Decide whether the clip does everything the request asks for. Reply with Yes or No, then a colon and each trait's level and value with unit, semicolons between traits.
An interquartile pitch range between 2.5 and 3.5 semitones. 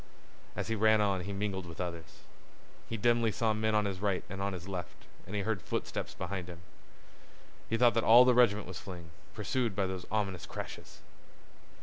Yes: average, 3.0 semitones